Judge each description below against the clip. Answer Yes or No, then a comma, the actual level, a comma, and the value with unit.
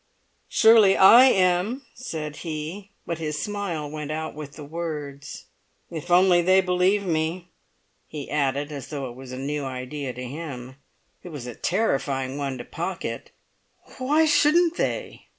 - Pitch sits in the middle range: Yes, medium, 155 Hz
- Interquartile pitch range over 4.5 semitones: Yes, average, 4.9 semitones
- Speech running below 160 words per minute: Yes, average, 150 wpm